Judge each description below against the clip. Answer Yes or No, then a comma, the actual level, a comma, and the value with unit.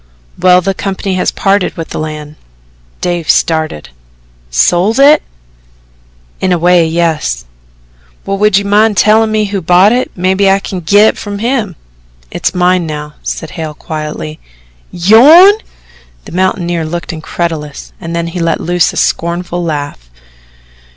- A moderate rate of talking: Yes, average, 145 wpm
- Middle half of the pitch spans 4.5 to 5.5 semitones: No, average, 3.7 semitones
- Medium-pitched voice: Yes, medium, 175 Hz